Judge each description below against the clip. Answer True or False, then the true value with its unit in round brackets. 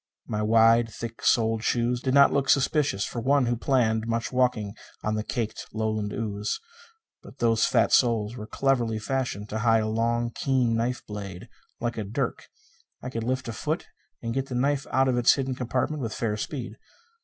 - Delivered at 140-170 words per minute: False (190 wpm)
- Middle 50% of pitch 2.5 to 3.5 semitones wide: True (2.8 semitones)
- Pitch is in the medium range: False (115 Hz)